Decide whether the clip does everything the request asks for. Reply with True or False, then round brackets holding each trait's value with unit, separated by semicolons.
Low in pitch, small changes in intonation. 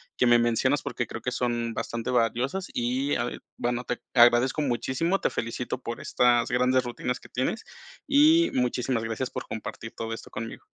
True (120 Hz; 1.7 semitones)